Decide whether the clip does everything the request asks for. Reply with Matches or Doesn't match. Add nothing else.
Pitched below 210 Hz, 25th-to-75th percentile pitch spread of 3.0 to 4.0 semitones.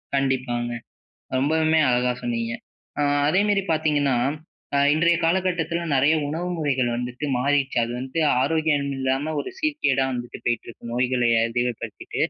Doesn't match